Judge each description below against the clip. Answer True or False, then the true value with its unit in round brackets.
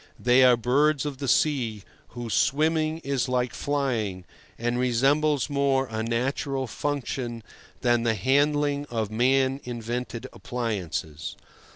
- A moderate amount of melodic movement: True (3.2 semitones)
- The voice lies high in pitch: False (125 Hz)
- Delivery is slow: True (125 wpm)